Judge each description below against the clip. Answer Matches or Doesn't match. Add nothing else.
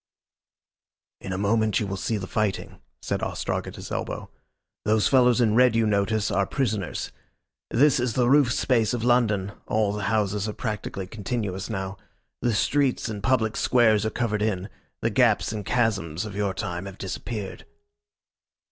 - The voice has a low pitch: Matches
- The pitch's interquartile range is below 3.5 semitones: Matches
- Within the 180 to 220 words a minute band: Doesn't match